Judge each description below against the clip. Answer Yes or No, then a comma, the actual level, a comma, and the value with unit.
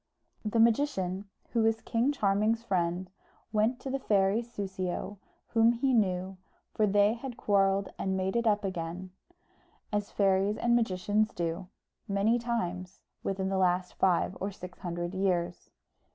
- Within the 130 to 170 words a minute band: Yes, average, 145 wpm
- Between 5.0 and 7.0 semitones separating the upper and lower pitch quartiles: No, average, 3.3 semitones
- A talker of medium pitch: No, high, 195 Hz